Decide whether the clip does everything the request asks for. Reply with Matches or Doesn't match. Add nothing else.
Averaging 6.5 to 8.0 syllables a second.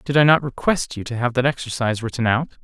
Matches